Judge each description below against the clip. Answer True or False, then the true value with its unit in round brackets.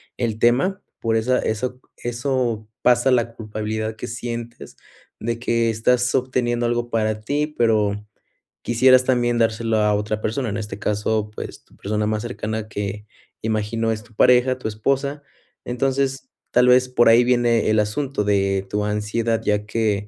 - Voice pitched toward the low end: True (115 Hz)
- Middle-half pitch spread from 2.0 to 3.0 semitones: True (2.5 semitones)